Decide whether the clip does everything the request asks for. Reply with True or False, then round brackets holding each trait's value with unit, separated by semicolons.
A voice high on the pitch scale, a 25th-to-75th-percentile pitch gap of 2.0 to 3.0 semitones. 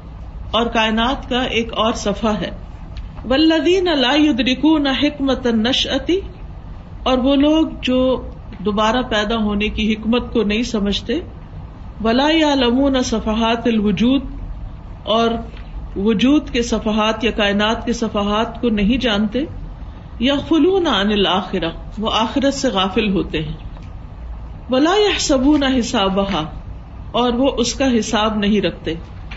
False (225 Hz; 4.2 semitones)